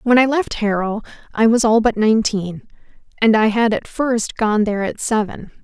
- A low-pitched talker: No, high, 220 Hz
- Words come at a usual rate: Yes, average, 190 wpm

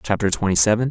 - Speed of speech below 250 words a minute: Yes, average, 200 wpm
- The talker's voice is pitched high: No, low, 105 Hz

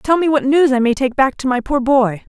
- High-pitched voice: Yes, very high, 265 Hz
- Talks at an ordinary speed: No, fast, 305 wpm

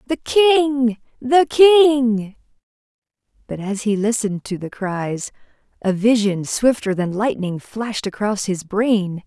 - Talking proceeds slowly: Yes, slow, 130 wpm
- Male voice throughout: No, female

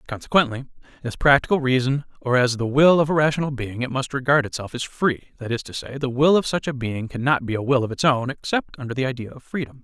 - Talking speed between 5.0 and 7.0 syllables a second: Yes, 6.2 syllables/s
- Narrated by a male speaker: Yes, male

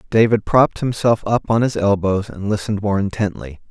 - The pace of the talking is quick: No, average, 180 wpm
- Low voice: Yes, low, 105 Hz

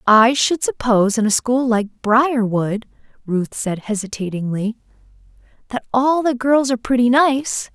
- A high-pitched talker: Yes, high, 235 Hz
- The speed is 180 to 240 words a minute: No, average, 140 wpm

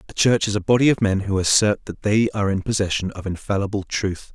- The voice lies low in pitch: Yes, low, 100 Hz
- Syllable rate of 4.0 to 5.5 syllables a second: No, 6.0 syllables/s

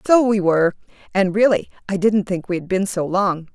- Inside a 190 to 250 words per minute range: Yes, fast, 205 wpm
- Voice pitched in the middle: No, high, 195 Hz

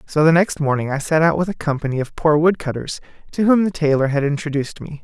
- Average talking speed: No, fast, 250 wpm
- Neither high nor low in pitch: Yes, medium, 155 Hz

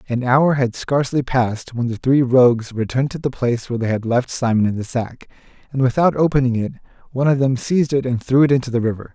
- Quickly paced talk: Yes, fast, 235 wpm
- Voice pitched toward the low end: Yes, low, 125 Hz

